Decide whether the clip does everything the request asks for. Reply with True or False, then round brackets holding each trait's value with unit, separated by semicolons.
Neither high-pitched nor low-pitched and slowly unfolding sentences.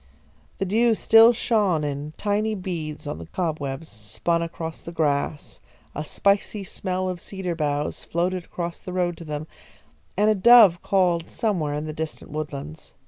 False (170 Hz; 160 wpm)